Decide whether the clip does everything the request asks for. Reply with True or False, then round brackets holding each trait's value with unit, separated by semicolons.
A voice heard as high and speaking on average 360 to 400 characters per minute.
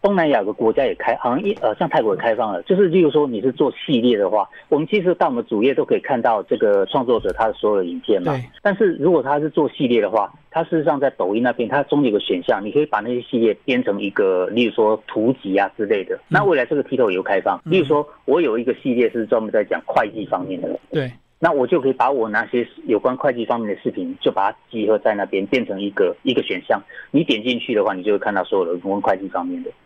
True (210 Hz; 380 characters per minute)